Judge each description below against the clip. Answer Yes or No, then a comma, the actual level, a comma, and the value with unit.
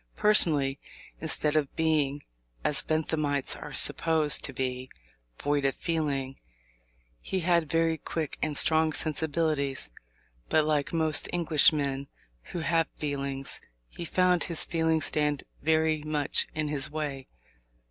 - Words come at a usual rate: No, slow, 125 wpm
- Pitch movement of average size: No, narrow, 2.2 semitones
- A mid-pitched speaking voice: Yes, medium, 155 Hz